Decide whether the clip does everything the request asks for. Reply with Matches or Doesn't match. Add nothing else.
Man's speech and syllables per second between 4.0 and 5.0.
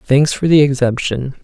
Matches